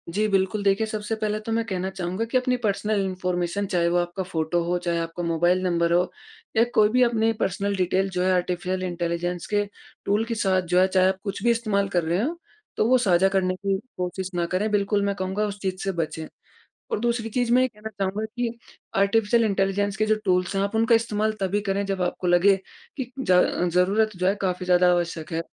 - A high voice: Yes, high, 195 Hz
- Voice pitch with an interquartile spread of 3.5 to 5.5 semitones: No, average, 3.0 semitones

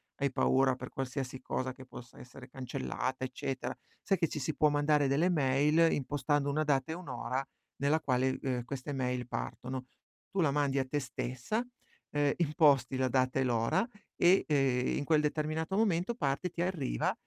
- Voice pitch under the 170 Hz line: Yes, medium, 140 Hz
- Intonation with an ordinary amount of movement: Yes, average, 3.0 semitones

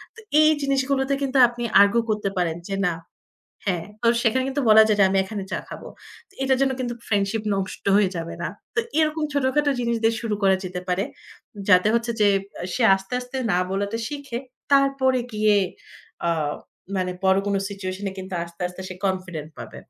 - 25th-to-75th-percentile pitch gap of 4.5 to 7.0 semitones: Yes, wide, 5.6 semitones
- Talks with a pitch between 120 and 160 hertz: No, high, 210 Hz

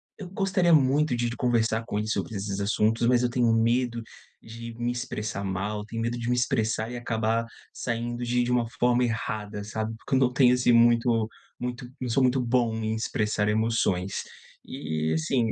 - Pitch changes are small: Yes, narrow, 2.1 semitones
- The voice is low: Yes, low, 115 Hz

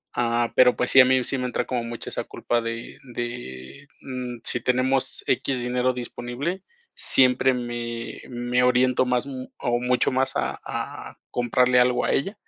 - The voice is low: Yes, low, 125 Hz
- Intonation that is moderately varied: No, narrow, 1.2 semitones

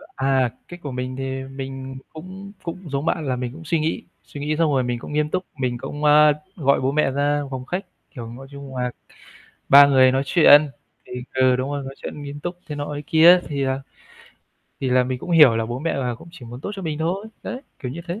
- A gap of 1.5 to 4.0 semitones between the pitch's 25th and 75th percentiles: Yes, average, 3.2 semitones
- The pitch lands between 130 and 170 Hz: Yes, medium, 140 Hz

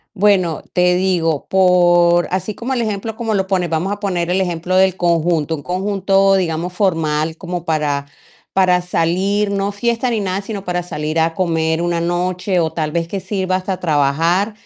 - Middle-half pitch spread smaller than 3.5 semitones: Yes, average, 2.8 semitones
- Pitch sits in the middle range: Yes, medium, 180 Hz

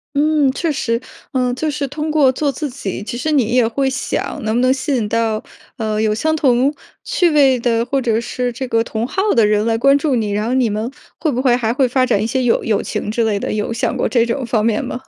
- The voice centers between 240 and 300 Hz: Yes, high, 245 Hz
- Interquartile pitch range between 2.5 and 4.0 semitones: Yes, average, 3.4 semitones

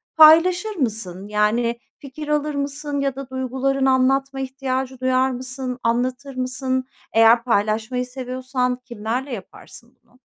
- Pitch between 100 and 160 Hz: No, very high, 255 Hz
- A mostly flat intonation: Yes, narrow, 2.0 semitones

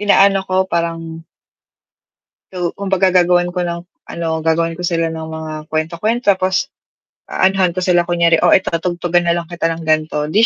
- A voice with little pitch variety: Yes, narrow, 2.0 semitones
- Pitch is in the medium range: Yes, medium, 175 Hz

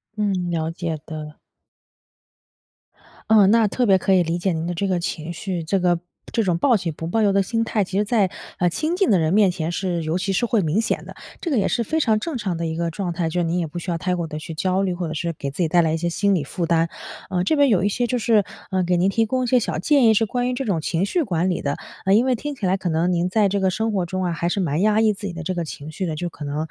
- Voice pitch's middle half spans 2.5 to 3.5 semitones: No, average, 4.1 semitones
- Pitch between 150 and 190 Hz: Yes, medium, 185 Hz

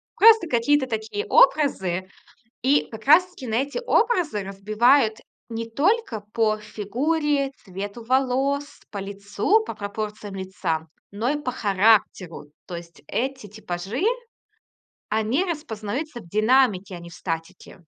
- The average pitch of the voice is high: Yes, high, 220 Hz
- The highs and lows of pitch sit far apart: Yes, wide, 5.8 semitones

